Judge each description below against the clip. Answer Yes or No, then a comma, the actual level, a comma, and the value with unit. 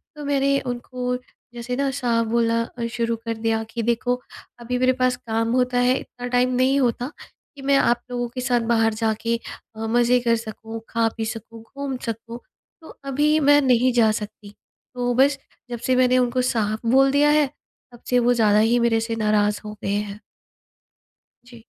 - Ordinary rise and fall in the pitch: No, narrow, 2.0 semitones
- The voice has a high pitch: Yes, high, 240 Hz